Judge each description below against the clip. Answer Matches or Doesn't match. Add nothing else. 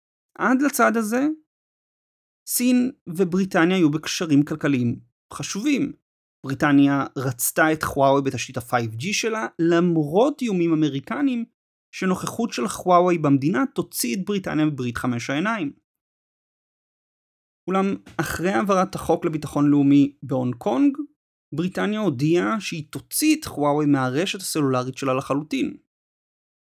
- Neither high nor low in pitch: Matches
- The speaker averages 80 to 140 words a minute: Matches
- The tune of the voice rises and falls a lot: Matches